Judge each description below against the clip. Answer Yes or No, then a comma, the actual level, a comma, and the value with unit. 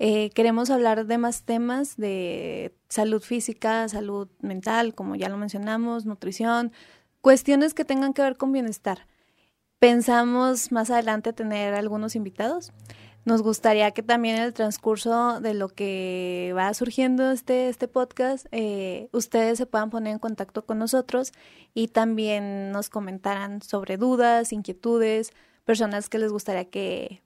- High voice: Yes, high, 225 Hz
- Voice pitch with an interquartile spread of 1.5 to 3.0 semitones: Yes, narrow, 2.6 semitones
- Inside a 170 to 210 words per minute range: No, average, 145 wpm